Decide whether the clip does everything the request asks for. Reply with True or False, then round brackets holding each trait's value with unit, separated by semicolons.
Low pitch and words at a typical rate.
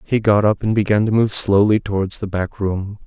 False (105 Hz; 235 wpm)